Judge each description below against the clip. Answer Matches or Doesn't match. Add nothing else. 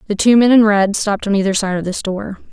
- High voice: Matches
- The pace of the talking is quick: Matches